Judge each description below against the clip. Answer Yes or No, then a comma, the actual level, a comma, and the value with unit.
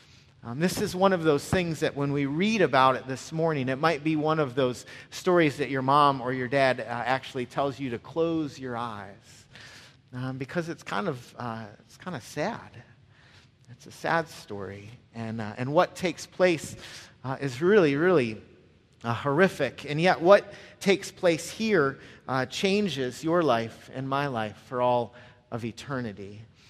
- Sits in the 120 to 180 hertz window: Yes, low, 135 Hz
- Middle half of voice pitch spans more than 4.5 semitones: Yes, average, 5.1 semitones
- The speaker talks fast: No, average, 180 wpm